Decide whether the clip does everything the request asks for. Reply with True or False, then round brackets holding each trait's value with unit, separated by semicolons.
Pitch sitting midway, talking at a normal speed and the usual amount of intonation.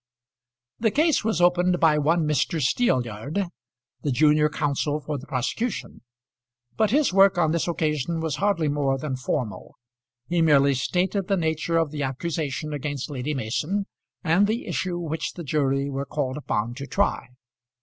True (155 Hz; 160 wpm; 4.0 semitones)